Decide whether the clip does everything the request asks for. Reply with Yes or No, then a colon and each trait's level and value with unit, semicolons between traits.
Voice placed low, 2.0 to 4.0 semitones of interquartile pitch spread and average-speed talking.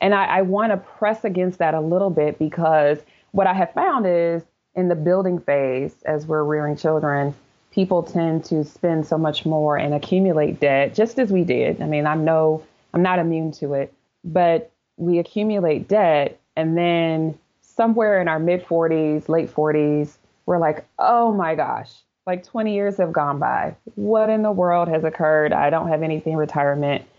No: medium, 165 Hz; average, 3.2 semitones; average, 190 wpm